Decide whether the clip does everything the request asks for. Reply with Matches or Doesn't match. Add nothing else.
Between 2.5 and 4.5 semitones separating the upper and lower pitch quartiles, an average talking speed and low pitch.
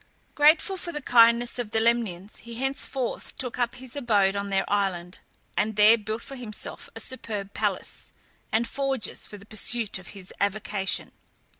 Doesn't match